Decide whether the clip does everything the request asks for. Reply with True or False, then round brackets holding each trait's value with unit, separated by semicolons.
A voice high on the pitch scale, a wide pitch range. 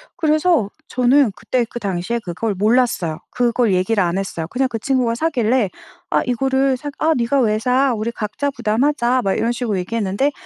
False (235 Hz; 4.0 semitones)